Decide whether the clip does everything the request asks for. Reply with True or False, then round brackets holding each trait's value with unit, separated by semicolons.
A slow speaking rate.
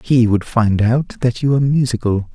False (205 wpm)